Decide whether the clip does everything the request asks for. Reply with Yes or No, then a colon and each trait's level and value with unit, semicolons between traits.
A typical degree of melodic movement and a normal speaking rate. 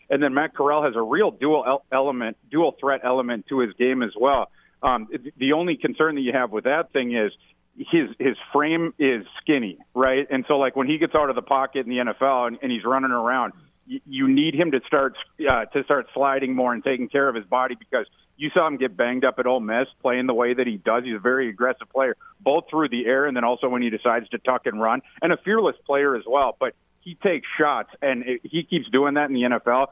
No: average, 3.4 semitones; fast, 245 wpm